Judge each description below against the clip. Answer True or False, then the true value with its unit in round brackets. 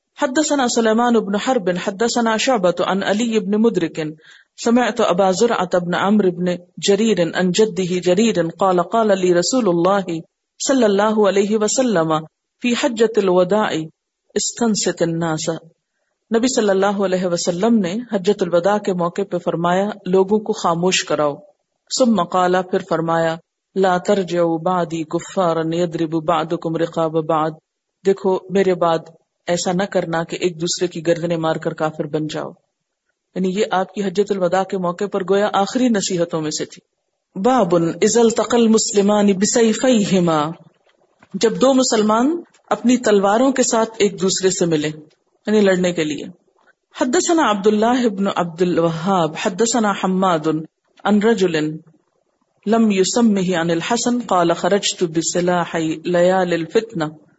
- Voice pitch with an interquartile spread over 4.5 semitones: False (4.2 semitones)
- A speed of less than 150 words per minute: True (135 wpm)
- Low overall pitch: False (190 Hz)